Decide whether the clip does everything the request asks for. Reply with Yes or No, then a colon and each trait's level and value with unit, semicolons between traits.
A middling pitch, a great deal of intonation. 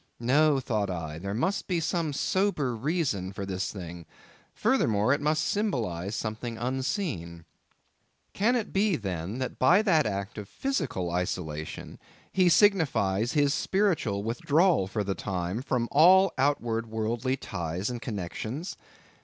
No: low, 120 Hz; wide, 8.2 semitones